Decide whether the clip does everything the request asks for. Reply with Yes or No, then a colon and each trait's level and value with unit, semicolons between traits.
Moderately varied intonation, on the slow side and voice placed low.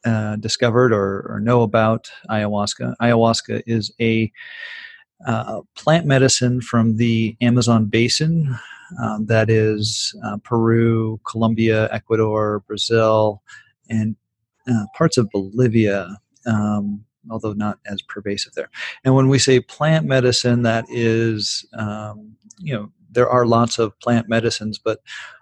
No: narrow, 2.3 semitones; slow, 125 wpm; low, 115 Hz